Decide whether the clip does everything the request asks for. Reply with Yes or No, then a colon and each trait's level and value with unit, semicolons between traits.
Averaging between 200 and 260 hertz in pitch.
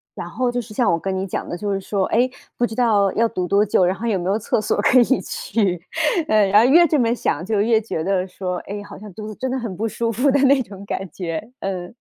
Yes: high, 210 Hz